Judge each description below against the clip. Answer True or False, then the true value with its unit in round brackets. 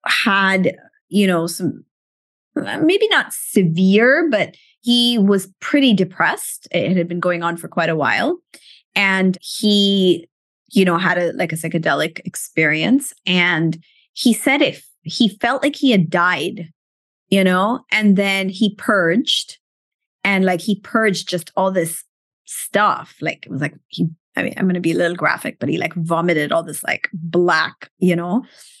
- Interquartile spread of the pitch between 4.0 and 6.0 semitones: True (4.9 semitones)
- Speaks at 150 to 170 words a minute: True (165 wpm)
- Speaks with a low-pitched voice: False (190 Hz)